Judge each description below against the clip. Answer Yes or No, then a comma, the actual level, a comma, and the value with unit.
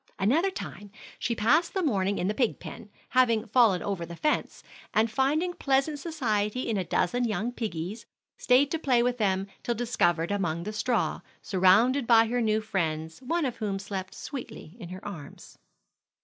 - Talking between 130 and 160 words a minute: No, average, 175 wpm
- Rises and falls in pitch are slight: No, average, 4.7 semitones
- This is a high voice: Yes, high, 220 Hz